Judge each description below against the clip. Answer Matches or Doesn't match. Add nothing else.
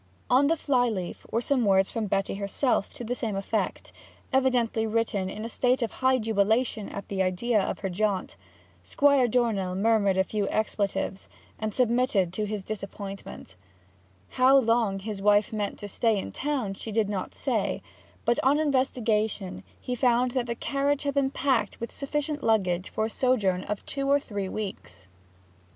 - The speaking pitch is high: Matches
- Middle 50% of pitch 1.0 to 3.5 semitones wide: Doesn't match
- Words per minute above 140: Matches